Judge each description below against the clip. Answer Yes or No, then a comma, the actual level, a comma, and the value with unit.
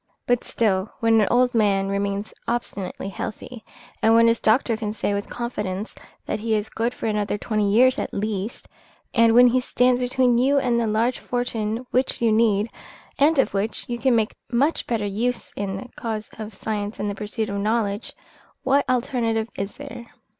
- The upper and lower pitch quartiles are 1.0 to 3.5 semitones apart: Yes, average, 2.8 semitones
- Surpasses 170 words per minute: Yes, average, 180 wpm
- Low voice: No, high, 225 Hz